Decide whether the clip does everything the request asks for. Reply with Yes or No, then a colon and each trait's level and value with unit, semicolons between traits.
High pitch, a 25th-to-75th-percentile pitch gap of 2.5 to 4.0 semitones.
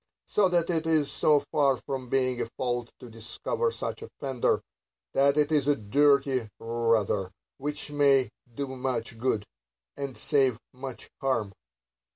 No: low, 135 Hz; average, 3.2 semitones